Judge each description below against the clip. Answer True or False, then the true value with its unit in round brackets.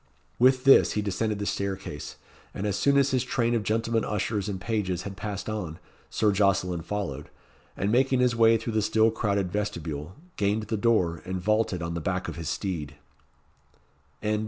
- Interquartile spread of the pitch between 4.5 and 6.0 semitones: False (3.4 semitones)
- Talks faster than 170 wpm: True (180 wpm)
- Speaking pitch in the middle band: False (105 Hz)